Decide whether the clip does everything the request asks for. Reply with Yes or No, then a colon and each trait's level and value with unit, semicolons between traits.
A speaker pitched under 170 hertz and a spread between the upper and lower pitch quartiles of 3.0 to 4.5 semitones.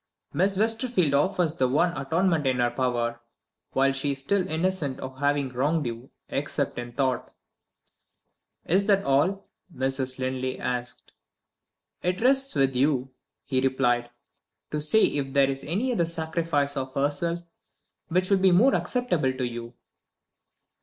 No: medium, 140 Hz; average, 5.3 semitones